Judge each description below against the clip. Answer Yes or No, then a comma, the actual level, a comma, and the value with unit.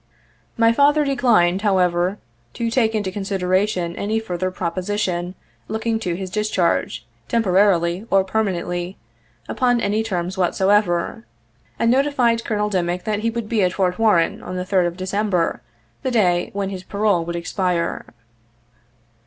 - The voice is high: Yes, high, 195 Hz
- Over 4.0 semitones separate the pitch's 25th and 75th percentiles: No, average, 3.6 semitones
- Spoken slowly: No, average, 145 wpm